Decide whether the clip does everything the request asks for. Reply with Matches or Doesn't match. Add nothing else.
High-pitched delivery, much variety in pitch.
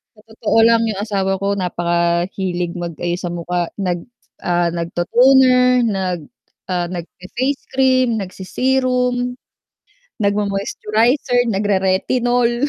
Matches